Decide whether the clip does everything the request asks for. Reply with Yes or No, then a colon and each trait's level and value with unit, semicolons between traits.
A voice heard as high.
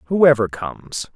No: low, 125 Hz